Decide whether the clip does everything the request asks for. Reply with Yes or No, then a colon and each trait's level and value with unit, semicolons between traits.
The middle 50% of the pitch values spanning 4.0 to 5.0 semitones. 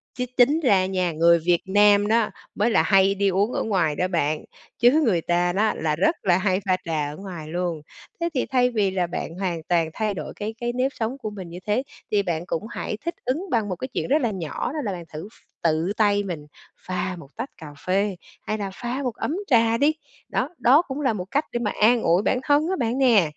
No: wide, 5.4 semitones